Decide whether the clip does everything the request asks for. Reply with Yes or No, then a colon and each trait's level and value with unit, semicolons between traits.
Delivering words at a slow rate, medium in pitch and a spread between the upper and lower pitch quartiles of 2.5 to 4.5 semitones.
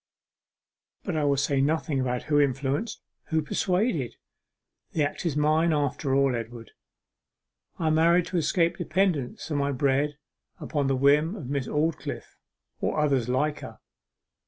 No: average, 145 wpm; medium, 145 Hz; average, 2.9 semitones